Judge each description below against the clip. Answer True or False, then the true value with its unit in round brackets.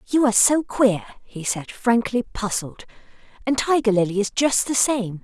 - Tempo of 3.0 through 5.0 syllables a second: True (4.5 syllables/s)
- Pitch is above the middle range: True (230 Hz)